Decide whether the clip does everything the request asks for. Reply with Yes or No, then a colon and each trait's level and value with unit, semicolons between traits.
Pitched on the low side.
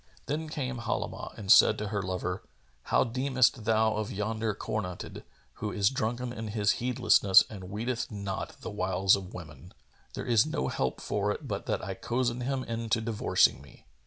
Yes: low, 110 Hz